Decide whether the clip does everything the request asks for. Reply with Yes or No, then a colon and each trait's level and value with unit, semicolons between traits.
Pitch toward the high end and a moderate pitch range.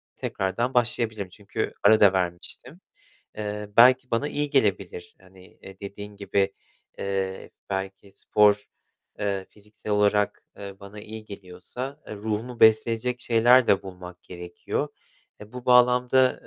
No: low, 105 Hz; average, 3.5 semitones